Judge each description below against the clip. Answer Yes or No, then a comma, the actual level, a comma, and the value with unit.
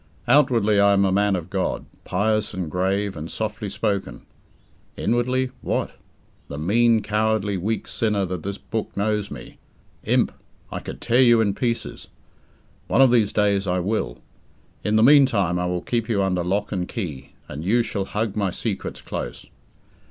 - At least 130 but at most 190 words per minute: Yes, average, 160 wpm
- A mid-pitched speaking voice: No, low, 100 Hz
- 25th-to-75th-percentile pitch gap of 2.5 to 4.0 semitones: Yes, average, 2.9 semitones